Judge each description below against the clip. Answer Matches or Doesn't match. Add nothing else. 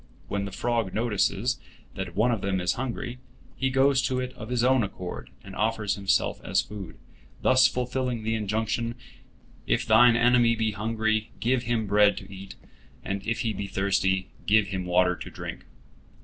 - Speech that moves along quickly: Doesn't match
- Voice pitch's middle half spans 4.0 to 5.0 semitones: Doesn't match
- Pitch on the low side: Matches